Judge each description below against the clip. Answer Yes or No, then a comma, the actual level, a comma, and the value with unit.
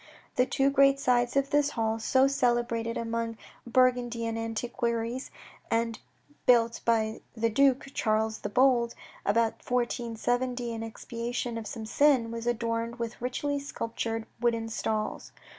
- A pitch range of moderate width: No, narrow, 1.7 semitones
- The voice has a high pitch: Yes, high, 235 Hz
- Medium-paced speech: No, slow, 130 wpm